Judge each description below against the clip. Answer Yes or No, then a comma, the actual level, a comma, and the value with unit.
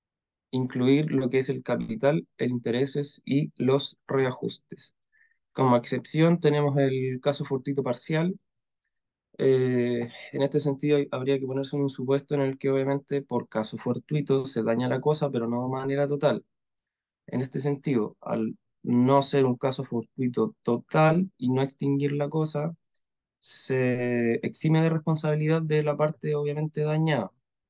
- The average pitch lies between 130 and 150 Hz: Yes, medium, 140 Hz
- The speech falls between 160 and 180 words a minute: No, average, 145 wpm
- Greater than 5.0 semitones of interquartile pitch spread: No, narrow, 2.6 semitones